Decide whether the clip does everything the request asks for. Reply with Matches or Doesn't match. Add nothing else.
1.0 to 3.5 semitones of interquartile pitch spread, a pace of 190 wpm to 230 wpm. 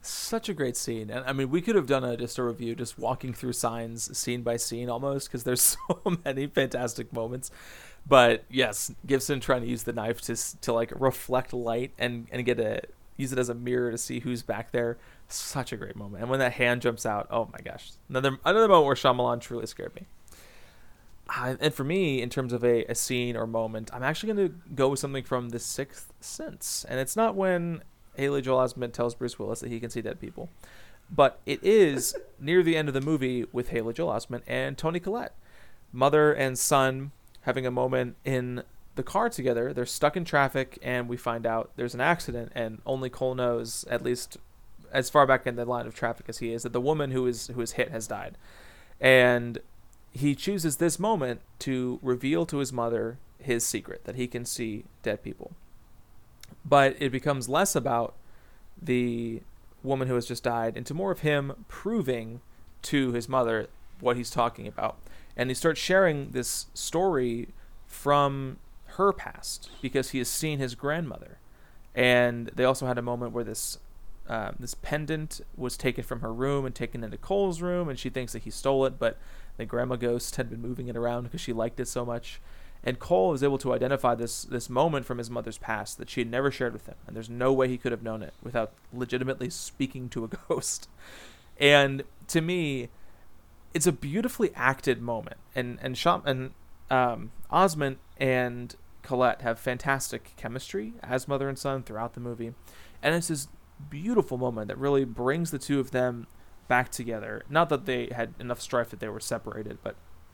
Matches